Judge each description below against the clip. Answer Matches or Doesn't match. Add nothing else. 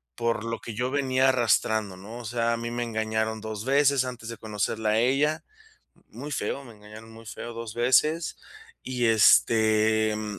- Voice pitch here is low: Matches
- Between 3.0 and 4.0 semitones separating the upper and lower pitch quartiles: Doesn't match